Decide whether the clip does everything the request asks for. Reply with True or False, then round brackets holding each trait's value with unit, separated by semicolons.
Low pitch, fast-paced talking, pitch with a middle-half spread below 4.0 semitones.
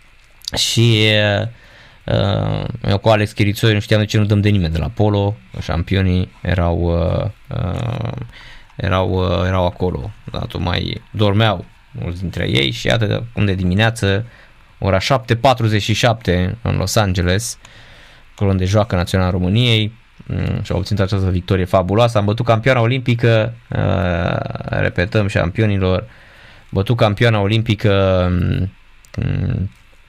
False (105 Hz; 135 wpm; 3.5 semitones)